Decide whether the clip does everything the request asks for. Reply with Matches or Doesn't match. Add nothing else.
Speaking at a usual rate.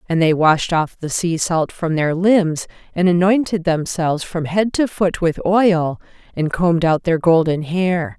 Matches